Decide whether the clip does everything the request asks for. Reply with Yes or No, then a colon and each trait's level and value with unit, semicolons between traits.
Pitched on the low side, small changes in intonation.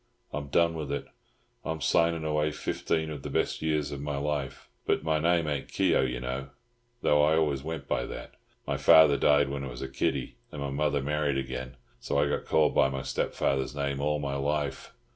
Yes: very low, 70 Hz; narrow, 2.0 semitones